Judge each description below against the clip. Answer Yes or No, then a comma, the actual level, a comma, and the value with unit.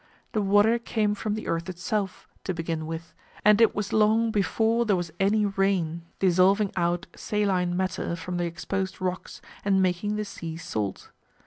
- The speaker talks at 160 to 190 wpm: Yes, average, 165 wpm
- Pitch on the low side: No, high, 190 Hz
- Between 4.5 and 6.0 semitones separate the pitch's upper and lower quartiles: No, average, 3.3 semitones